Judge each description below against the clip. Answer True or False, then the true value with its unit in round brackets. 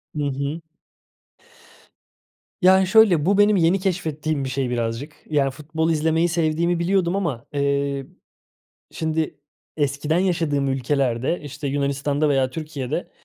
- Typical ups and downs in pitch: True (3.4 semitones)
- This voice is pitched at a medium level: True (150 Hz)